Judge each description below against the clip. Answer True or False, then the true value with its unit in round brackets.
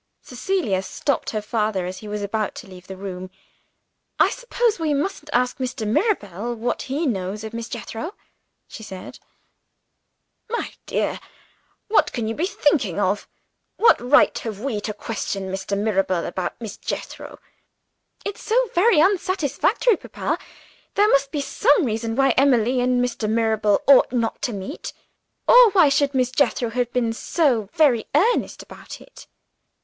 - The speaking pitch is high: True (240 Hz)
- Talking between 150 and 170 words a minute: True (155 wpm)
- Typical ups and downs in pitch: False (5.9 semitones)